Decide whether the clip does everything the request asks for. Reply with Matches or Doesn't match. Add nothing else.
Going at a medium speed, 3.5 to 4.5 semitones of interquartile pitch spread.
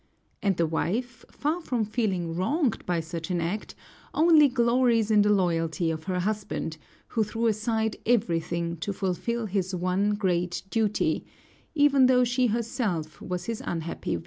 Doesn't match